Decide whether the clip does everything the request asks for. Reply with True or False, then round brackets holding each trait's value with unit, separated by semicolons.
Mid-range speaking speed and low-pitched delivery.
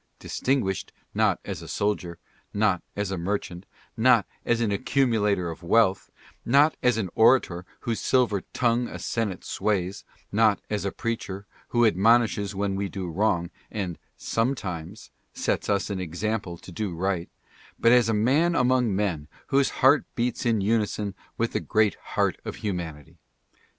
True (155 wpm; 105 Hz)